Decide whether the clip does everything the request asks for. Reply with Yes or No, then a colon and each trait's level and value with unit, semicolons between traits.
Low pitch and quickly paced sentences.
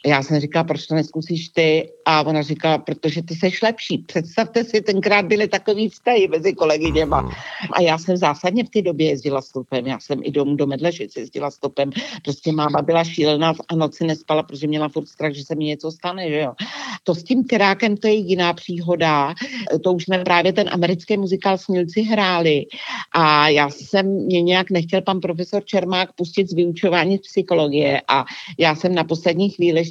No: medium, 170 Hz; fast, 190 wpm